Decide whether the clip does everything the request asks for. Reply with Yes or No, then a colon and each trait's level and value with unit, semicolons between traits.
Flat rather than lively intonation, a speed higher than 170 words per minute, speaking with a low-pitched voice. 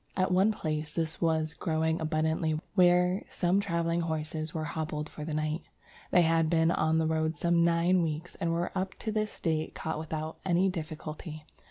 No: narrow, 1.9 semitones; average, 180 wpm; medium, 160 Hz